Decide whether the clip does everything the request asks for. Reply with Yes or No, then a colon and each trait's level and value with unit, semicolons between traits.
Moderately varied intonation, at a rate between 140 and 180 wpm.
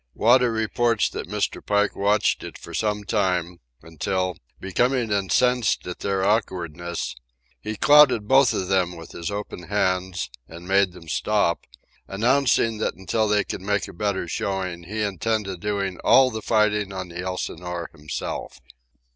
Yes: average, 3.2 semitones; average, 150 wpm